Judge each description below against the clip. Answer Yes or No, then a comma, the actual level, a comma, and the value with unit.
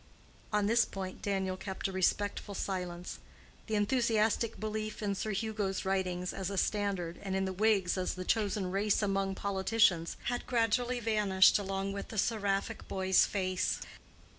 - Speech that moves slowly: No, average, 155 wpm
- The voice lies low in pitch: No, high, 200 Hz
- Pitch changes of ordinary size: No, narrow, 2.1 semitones